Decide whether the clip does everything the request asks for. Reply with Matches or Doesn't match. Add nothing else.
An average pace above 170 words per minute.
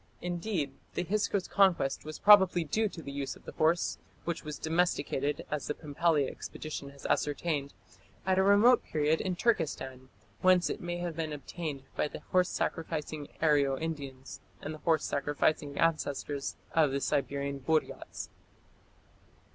Doesn't match